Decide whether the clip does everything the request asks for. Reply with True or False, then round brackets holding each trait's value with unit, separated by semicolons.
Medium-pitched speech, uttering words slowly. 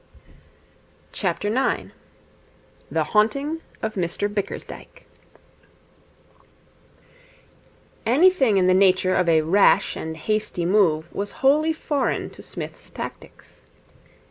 False (205 Hz; 90 wpm)